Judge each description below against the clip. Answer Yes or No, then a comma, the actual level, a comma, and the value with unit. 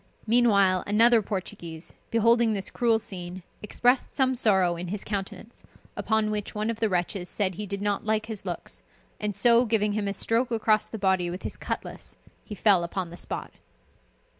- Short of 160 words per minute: No, average, 180 wpm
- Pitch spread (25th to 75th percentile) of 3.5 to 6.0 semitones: No, average, 3.0 semitones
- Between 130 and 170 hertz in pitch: No, high, 210 Hz